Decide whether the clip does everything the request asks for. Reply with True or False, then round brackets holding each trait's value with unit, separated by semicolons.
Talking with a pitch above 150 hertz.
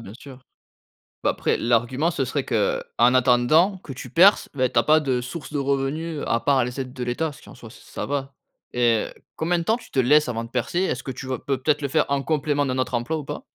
False (135 Hz)